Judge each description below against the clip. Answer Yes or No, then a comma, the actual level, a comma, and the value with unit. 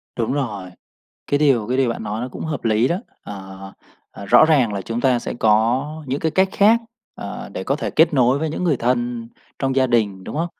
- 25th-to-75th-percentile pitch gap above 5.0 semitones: No, average, 4.7 semitones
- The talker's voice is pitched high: No, low, 125 Hz